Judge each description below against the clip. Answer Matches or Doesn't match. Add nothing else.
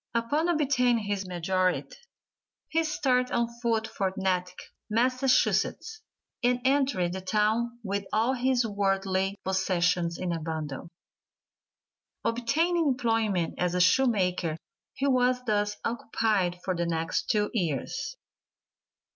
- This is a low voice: Doesn't match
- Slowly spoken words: Matches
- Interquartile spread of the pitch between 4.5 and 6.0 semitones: Matches